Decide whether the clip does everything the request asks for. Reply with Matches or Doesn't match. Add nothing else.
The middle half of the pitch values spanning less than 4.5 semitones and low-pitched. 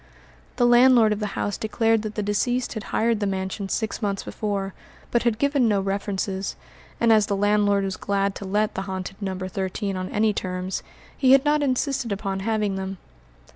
Doesn't match